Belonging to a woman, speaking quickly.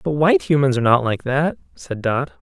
No: male; fast, 220 wpm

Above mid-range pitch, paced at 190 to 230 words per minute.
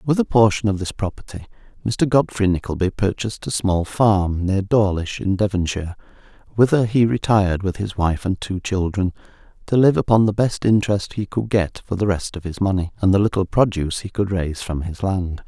No: low, 100 Hz; average, 200 wpm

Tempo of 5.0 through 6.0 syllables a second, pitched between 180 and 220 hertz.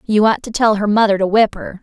Yes: 5.8 syllables/s; high, 210 Hz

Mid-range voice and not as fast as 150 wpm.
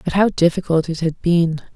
No: medium, 170 Hz; fast, 205 wpm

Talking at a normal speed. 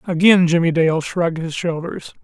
Yes: average, 160 wpm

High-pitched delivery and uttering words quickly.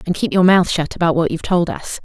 No: medium, 175 Hz; fast, 295 wpm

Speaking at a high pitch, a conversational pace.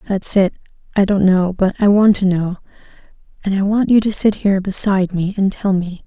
No: high, 195 Hz; fast, 220 wpm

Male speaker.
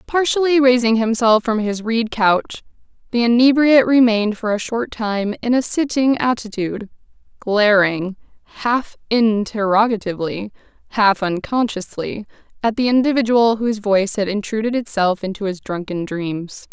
No: female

